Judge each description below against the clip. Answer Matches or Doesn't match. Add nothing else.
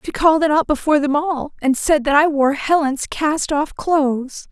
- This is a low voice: Doesn't match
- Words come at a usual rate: Doesn't match